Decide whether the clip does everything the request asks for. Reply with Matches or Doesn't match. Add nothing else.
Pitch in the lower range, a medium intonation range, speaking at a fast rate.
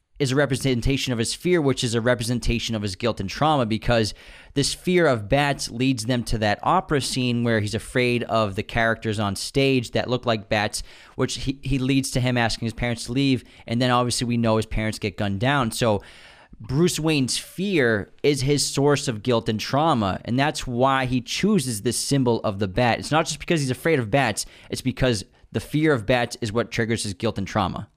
Matches